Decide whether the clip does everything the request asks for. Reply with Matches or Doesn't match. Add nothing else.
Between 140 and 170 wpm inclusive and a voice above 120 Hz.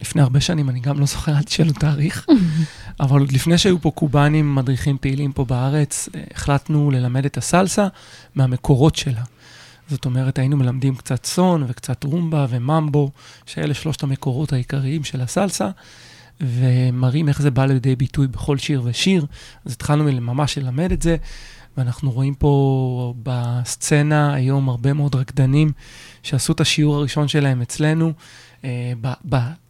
Matches